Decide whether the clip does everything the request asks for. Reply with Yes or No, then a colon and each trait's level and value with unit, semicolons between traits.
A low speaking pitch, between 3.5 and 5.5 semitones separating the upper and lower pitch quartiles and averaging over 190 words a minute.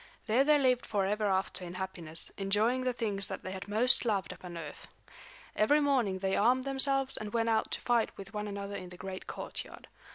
No: high, 210 Hz; average, 4.6 semitones; average, 200 wpm